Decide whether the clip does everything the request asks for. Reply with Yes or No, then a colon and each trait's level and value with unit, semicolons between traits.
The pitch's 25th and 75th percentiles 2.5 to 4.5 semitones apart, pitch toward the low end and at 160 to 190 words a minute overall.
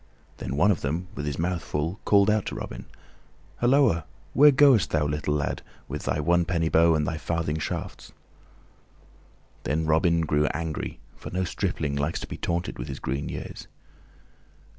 Yes: average, 3.4 semitones; very low, 80 Hz; average, 170 wpm